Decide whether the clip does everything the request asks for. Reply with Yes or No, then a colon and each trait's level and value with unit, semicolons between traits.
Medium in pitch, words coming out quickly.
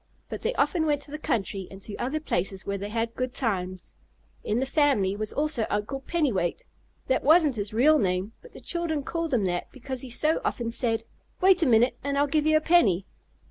No: very high, 255 Hz; fast, 215 wpm